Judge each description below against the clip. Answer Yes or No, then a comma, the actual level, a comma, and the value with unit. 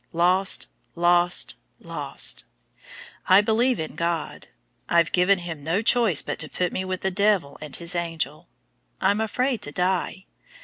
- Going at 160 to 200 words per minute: No, average, 145 wpm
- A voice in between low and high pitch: Yes, medium, 180 Hz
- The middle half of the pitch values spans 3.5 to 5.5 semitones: No, average, 2.9 semitones